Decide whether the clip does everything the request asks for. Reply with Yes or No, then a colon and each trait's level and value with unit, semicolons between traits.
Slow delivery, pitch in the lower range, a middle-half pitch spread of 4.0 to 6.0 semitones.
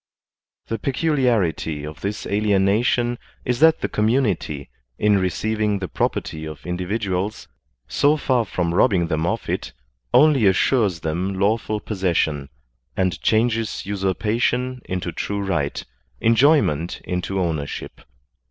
Yes: slow, 120 wpm; low, 100 Hz; average, 4.6 semitones